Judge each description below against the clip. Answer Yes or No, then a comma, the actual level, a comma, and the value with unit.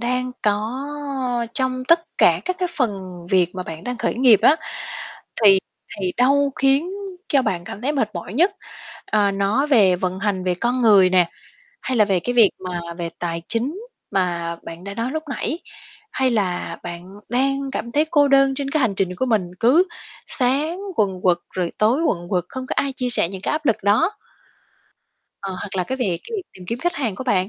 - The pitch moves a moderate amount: No, wide, 6.4 semitones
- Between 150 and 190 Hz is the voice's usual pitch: No, high, 225 Hz